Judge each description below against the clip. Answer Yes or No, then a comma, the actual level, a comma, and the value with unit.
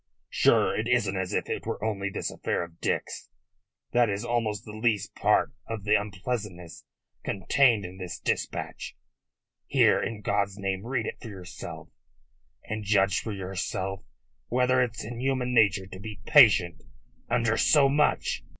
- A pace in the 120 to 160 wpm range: Yes, average, 155 wpm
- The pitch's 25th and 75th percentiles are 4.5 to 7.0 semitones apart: No, average, 3.6 semitones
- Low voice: Yes, low, 105 Hz